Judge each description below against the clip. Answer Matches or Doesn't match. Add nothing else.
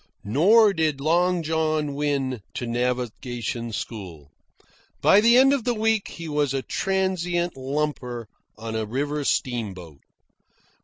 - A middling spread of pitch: Doesn't match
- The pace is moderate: Doesn't match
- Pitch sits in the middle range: Matches